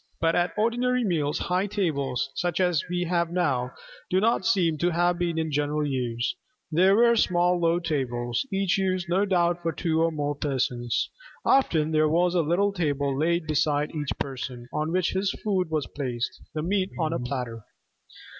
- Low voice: No, medium, 165 Hz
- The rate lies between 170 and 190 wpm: Yes, average, 180 wpm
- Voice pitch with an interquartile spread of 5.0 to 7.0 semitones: No, average, 3.8 semitones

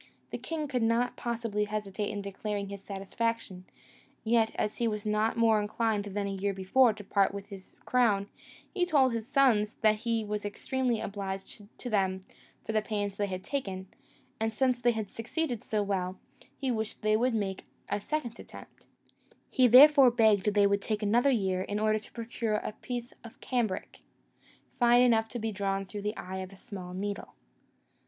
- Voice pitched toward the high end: Yes, high, 215 Hz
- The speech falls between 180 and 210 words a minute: Yes, average, 185 wpm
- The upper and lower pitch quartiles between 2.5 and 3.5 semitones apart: Yes, average, 2.9 semitones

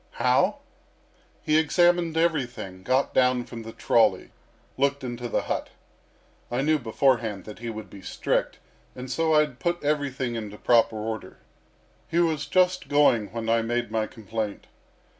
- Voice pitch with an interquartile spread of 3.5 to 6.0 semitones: Yes, average, 5.1 semitones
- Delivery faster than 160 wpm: No, average, 155 wpm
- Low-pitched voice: Yes, low, 125 Hz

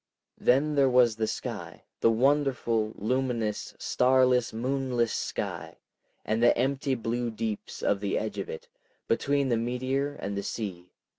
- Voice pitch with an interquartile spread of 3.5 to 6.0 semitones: No, average, 3.1 semitones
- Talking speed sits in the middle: Yes, average, 145 wpm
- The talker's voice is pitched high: No, low, 120 Hz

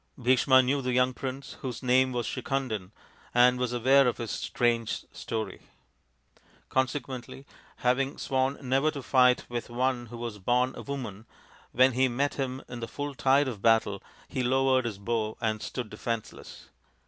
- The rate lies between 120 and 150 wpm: No, average, 165 wpm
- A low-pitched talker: Yes, low, 125 Hz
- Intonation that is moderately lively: No, narrow, 2.1 semitones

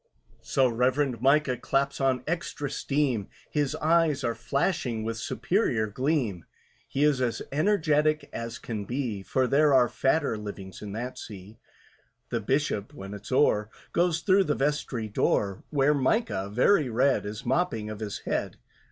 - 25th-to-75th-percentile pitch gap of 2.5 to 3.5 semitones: No, average, 5.2 semitones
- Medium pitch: No, low, 130 Hz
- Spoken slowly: No, average, 150 wpm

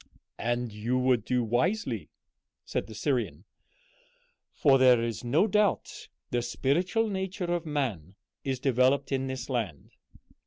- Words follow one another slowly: Yes, slow, 130 wpm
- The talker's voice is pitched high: No, low, 130 Hz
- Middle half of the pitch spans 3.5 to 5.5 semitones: Yes, average, 5.1 semitones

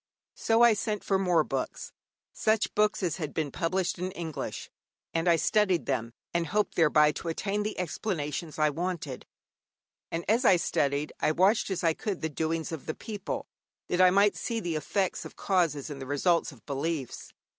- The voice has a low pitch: No, medium, 170 Hz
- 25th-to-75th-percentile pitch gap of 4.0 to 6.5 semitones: Yes, average, 4.4 semitones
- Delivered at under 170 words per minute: No, average, 185 wpm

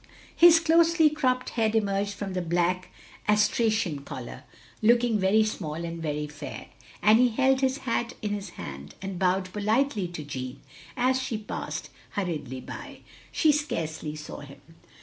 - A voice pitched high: Yes, high, 205 Hz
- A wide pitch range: Yes, wide, 6.5 semitones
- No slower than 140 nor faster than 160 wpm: Yes, average, 150 wpm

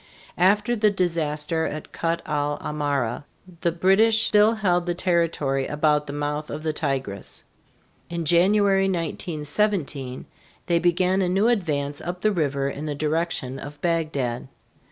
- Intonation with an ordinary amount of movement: Yes, average, 4.0 semitones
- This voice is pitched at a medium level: Yes, medium, 165 Hz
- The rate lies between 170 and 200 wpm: No, average, 140 wpm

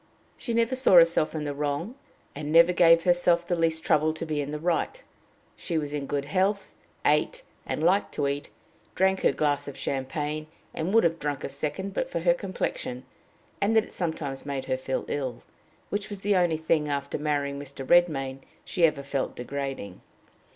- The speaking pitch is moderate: Yes, medium, 155 Hz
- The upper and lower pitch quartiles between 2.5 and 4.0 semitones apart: Yes, average, 3.7 semitones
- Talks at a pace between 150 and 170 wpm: No, average, 190 wpm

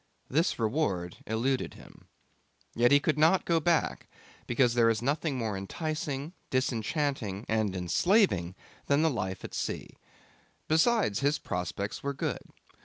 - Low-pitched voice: Yes, low, 130 Hz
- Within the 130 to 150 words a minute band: Yes, slow, 135 wpm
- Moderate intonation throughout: No, wide, 6.4 semitones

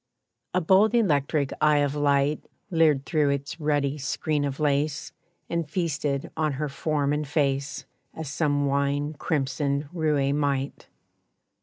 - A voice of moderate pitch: Yes, medium, 145 Hz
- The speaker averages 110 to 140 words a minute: Yes, slow, 135 wpm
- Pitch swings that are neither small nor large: No, narrow, 1.6 semitones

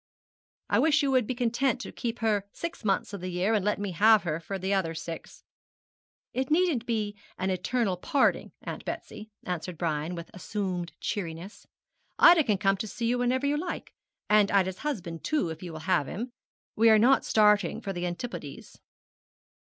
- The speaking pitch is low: No, high, 205 Hz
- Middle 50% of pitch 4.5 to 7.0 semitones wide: Yes, average, 5.2 semitones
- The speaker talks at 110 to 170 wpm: No, average, 185 wpm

